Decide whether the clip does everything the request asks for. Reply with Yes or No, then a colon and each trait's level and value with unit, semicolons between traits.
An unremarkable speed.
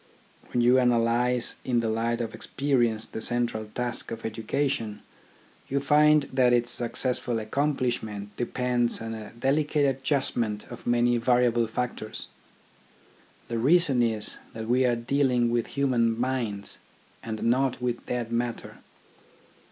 No: slow, 130 wpm